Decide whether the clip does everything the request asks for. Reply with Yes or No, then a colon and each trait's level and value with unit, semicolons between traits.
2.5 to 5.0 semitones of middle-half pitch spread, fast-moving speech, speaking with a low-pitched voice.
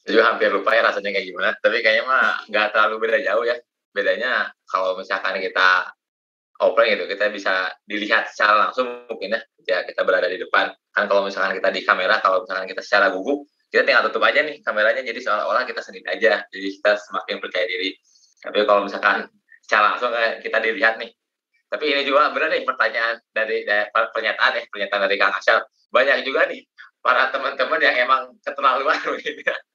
No: wide, 5.4 semitones; fast, 180 wpm; low, 115 Hz